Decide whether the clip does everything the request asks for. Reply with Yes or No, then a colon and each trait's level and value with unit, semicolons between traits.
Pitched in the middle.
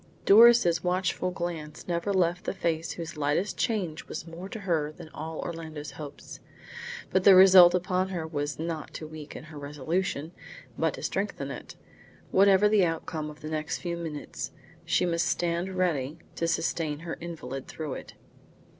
Yes: medium, 165 Hz